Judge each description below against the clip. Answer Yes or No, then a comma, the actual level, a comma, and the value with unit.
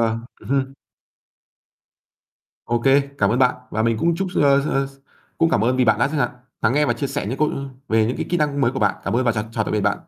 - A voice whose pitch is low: Yes, low, 130 Hz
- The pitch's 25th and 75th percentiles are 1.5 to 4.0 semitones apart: Yes, average, 3.7 semitones